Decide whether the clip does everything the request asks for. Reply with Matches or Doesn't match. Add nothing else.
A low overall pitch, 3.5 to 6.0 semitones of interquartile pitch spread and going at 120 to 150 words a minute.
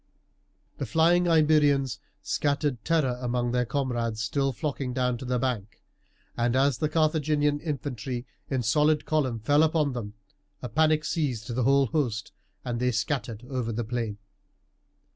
Matches